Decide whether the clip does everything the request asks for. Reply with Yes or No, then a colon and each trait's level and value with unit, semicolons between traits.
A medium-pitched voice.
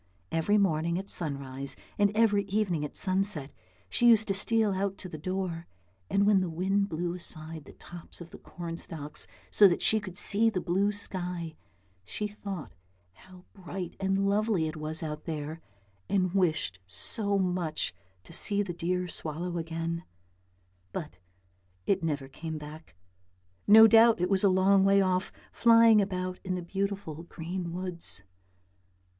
Yes: medium, 180 Hz